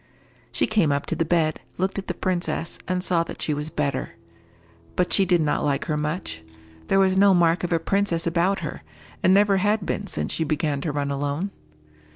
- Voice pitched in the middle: Yes, medium, 170 Hz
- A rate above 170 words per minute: Yes, fast, 205 wpm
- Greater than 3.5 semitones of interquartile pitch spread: Yes, average, 4.1 semitones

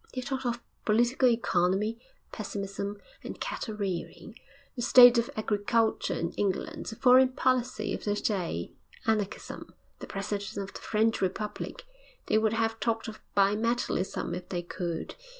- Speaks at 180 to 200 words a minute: No, average, 150 wpm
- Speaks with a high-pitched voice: Yes, high, 215 Hz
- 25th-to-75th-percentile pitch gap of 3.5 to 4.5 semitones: No, average, 3.0 semitones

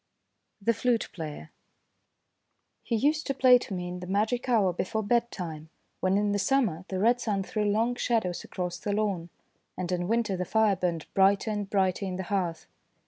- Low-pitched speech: No, high, 200 Hz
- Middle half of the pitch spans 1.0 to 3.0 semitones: No, average, 3.9 semitones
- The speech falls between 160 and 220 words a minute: Yes, average, 185 wpm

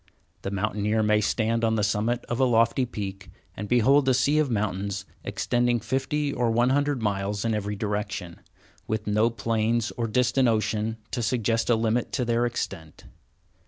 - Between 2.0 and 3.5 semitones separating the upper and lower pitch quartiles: Yes, narrow, 2.5 semitones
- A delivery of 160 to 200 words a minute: Yes, average, 170 wpm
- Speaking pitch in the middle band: No, low, 115 Hz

